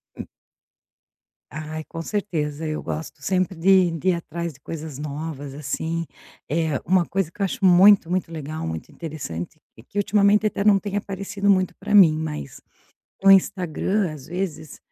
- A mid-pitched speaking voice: Yes, medium, 170 Hz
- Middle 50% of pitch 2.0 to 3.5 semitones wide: No, average, 4.0 semitones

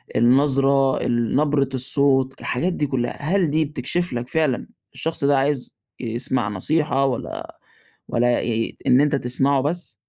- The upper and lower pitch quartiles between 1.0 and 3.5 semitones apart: Yes, average, 3.2 semitones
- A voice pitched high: No, low, 135 Hz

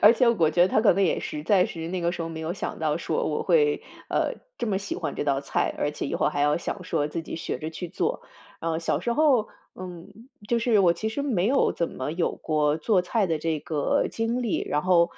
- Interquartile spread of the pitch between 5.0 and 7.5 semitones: Yes, wide, 5.5 semitones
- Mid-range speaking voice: Yes, medium, 175 Hz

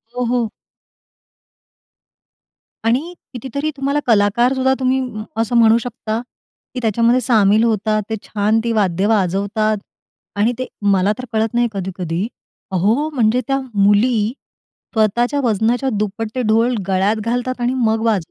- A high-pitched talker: Yes, high, 225 Hz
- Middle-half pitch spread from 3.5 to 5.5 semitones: No, average, 3.1 semitones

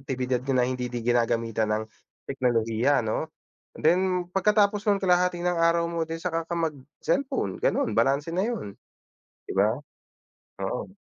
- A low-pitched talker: No, medium, 160 Hz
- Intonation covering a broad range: Yes, wide, 6.6 semitones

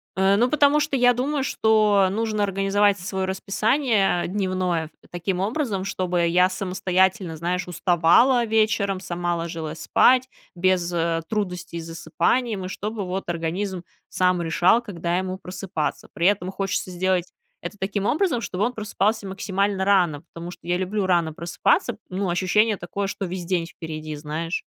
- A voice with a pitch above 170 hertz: Yes, high, 190 Hz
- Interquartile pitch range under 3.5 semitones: Yes, average, 2.9 semitones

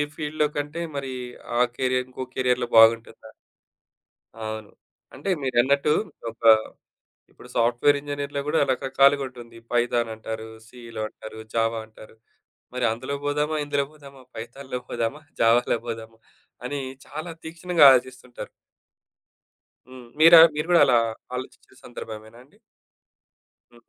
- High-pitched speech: No, low, 130 Hz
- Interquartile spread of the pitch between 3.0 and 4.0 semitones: Yes, average, 3.6 semitones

